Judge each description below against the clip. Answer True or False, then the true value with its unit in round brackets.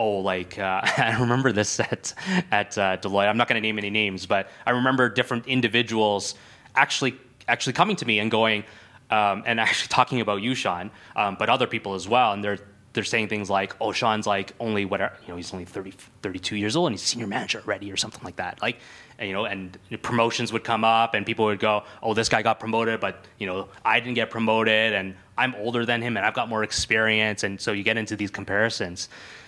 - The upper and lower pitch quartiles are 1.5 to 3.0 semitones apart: True (2.7 semitones)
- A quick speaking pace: True (230 wpm)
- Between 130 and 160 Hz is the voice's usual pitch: False (110 Hz)